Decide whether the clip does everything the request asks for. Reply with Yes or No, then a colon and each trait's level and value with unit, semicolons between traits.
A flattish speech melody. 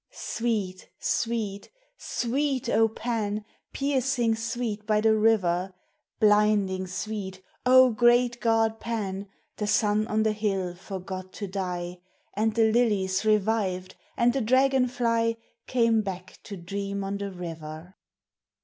No: average, 3.3 semitones